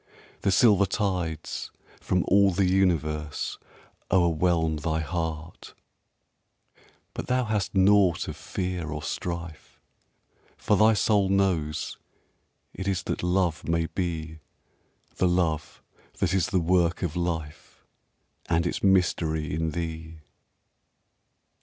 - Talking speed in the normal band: No, slow, 115 wpm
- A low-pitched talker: Yes, very low, 85 Hz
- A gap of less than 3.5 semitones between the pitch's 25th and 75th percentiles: Yes, average, 2.9 semitones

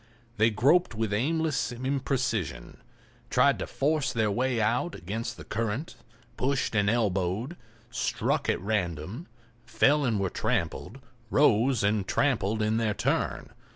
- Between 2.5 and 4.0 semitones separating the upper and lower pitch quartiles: No, average, 4.4 semitones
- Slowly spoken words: Yes, slow, 130 wpm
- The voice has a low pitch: Yes, low, 115 Hz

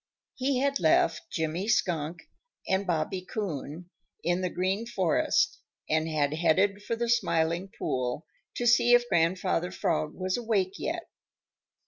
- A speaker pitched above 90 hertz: Yes, medium, 185 Hz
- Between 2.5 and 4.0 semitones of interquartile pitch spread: No, average, 5.2 semitones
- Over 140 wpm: No, slow, 135 wpm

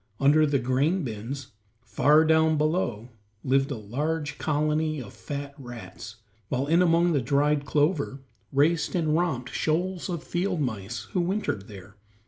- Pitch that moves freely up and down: No, average, 4.1 semitones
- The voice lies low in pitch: No, medium, 145 Hz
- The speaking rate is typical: Yes, average, 145 wpm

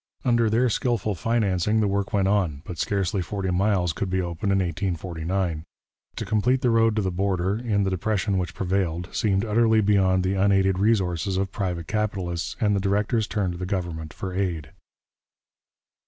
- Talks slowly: No, average, 175 wpm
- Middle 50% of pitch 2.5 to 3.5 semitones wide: Yes, average, 2.8 semitones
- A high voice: No, very low, 95 Hz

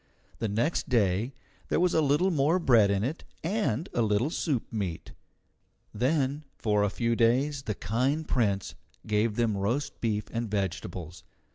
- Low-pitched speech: Yes, low, 115 Hz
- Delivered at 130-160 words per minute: Yes, average, 155 wpm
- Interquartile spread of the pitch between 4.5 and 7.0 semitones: Yes, wide, 5.5 semitones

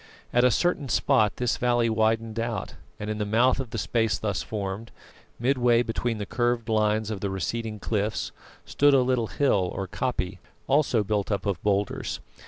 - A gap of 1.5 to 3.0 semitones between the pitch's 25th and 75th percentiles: Yes, average, 2.7 semitones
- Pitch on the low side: Yes, low, 110 Hz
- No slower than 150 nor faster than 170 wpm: No, average, 180 wpm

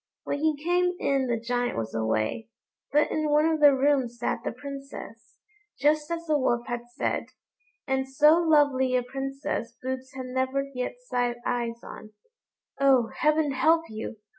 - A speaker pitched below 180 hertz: No, very high, 265 Hz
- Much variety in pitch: No, average, 3.6 semitones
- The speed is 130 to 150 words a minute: No, average, 165 wpm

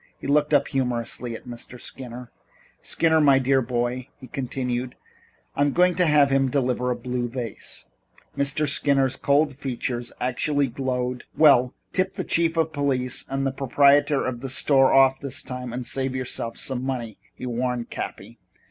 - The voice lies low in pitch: Yes, low, 130 Hz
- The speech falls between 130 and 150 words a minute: No, average, 165 wpm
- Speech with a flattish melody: Yes, narrow, 2.2 semitones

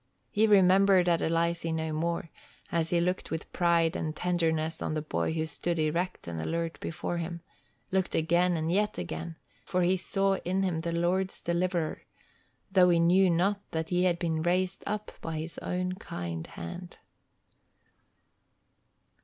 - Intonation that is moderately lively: No, narrow, 2.2 semitones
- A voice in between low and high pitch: Yes, medium, 170 Hz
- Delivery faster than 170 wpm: No, average, 155 wpm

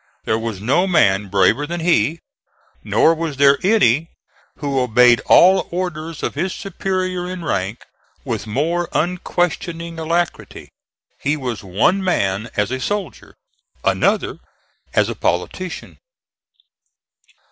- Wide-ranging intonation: Yes, wide, 7.1 semitones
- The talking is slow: Yes, slow, 120 wpm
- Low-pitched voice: No, medium, 155 Hz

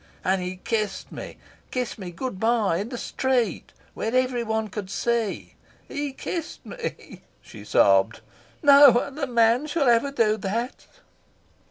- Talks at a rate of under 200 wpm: Yes, average, 145 wpm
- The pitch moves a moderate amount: Yes, average, 3.7 semitones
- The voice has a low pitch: No, high, 235 Hz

